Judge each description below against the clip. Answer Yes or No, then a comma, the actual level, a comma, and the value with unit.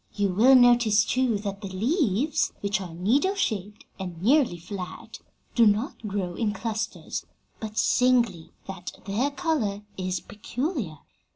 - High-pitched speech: Yes, high, 210 Hz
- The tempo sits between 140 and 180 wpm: Yes, average, 145 wpm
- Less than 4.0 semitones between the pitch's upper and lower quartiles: No, average, 4.5 semitones